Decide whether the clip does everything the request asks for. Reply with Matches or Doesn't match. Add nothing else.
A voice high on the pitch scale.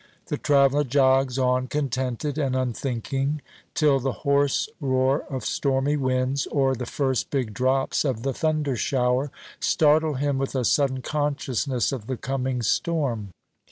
Doesn't match